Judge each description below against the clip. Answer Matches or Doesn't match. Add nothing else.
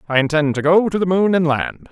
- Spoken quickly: Matches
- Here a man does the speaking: Matches